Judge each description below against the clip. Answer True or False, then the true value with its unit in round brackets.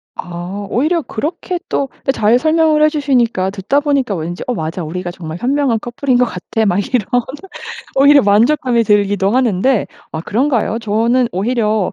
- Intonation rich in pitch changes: True (5.8 semitones)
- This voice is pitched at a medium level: False (235 Hz)